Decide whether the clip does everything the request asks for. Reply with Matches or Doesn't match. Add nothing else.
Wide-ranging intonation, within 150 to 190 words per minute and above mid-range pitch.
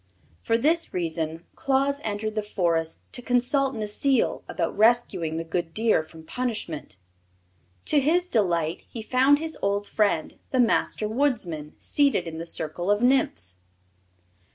Doesn't match